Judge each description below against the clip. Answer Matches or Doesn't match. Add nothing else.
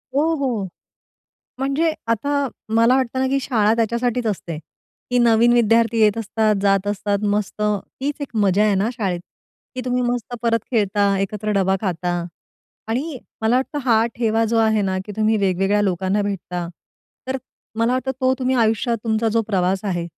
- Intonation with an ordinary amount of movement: Matches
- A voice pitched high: Matches